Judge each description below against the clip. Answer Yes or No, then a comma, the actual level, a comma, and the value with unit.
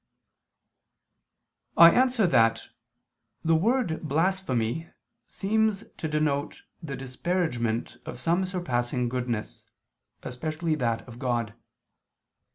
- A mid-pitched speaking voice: Yes, medium, 155 Hz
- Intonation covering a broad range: Yes, wide, 6.7 semitones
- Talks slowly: Yes, slow, 90 wpm